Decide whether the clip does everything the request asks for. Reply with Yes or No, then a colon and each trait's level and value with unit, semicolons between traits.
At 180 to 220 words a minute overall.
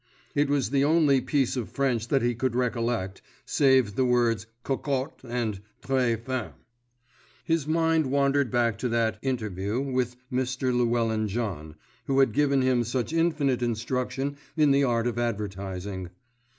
No: average, 150 wpm